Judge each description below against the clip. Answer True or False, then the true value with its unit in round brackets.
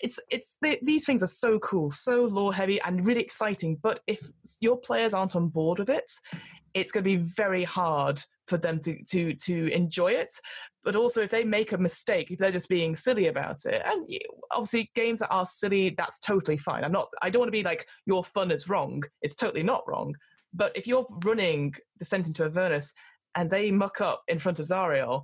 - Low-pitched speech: False (190 Hz)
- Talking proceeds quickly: True (215 wpm)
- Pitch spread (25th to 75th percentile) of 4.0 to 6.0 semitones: True (4.4 semitones)